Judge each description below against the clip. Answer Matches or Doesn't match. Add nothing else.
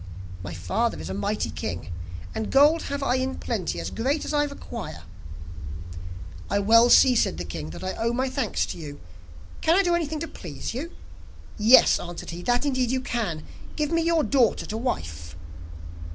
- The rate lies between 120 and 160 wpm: Doesn't match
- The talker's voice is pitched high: Matches